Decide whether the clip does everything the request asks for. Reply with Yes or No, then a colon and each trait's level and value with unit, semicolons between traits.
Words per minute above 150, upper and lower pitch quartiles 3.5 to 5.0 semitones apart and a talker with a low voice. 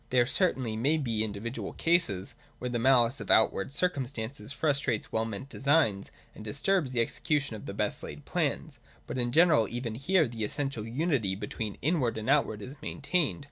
Yes: average, 180 wpm; average, 4.6 semitones; low, 125 Hz